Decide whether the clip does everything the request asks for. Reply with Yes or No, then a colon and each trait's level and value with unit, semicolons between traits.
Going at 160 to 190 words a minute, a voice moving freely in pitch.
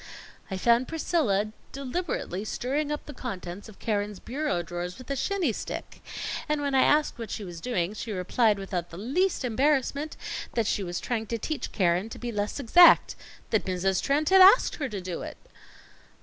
Yes: average, 185 wpm; wide, 6.7 semitones